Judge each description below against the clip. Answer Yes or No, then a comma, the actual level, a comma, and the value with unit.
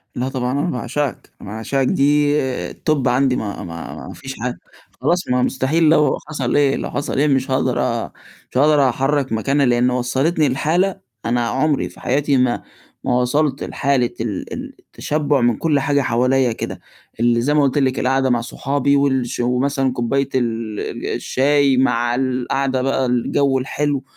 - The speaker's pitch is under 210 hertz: Yes, low, 135 Hz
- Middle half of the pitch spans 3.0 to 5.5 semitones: No, narrow, 2.4 semitones